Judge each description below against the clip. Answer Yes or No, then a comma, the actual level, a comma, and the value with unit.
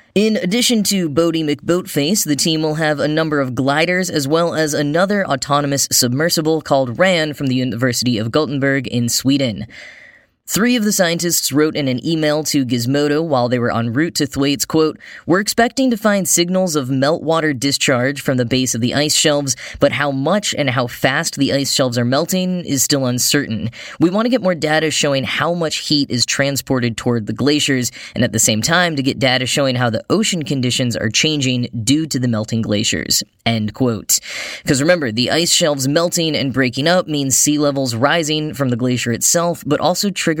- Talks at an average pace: Yes, average, 195 wpm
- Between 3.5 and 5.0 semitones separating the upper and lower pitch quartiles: Yes, average, 4.2 semitones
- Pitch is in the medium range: Yes, medium, 145 Hz